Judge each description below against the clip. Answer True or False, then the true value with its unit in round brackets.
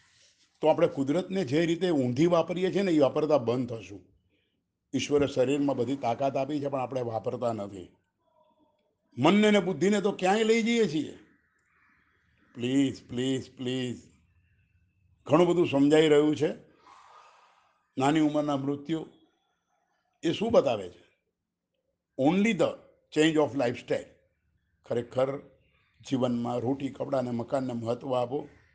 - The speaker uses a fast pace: False (120 wpm)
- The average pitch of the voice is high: False (135 Hz)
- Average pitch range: False (5.8 semitones)